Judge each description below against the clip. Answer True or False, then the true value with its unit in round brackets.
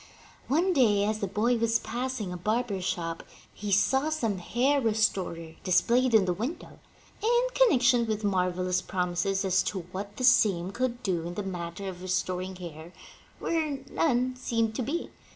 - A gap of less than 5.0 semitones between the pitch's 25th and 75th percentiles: False (5.3 semitones)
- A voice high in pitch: True (210 Hz)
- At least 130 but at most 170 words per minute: True (165 wpm)